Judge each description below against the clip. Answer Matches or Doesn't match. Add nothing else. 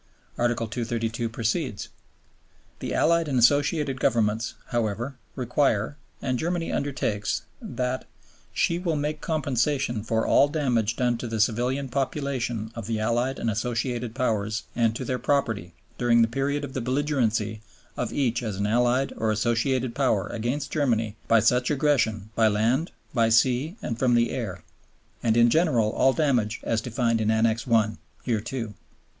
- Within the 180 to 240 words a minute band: Doesn't match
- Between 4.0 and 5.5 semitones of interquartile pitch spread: Doesn't match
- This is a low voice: Matches